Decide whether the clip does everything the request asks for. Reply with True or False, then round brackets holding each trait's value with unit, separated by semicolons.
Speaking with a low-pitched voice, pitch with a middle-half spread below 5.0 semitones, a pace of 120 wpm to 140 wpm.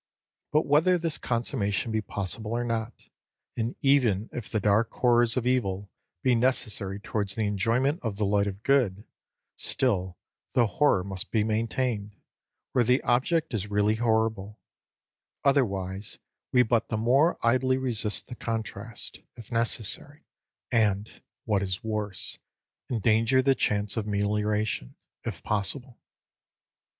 True (110 Hz; 3.3 semitones; 135 wpm)